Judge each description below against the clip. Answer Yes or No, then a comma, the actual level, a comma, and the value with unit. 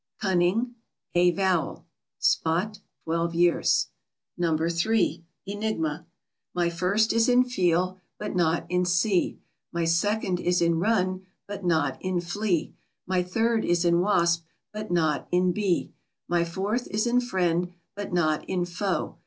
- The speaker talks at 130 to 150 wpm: Yes, average, 140 wpm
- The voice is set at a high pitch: No, medium, 180 Hz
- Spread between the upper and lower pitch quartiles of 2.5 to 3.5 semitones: Yes, average, 3.1 semitones